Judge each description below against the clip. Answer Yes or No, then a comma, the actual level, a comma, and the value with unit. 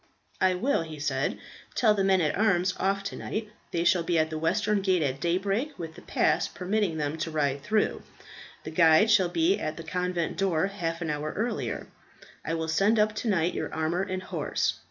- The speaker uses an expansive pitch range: No, average, 3.7 semitones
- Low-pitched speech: No, medium, 180 Hz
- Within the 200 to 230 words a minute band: Yes, fast, 205 wpm